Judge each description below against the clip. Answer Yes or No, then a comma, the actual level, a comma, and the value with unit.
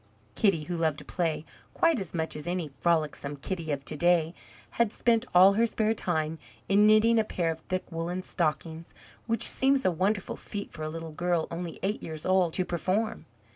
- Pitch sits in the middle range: Yes, medium, 175 Hz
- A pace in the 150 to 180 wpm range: No, average, 195 wpm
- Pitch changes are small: No, average, 4.0 semitones